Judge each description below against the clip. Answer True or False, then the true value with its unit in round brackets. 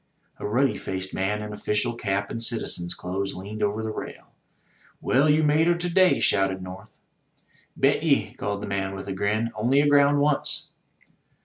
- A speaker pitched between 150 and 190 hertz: False (105 Hz)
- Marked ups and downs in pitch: True (6.3 semitones)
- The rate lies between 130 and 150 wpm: False (175 wpm)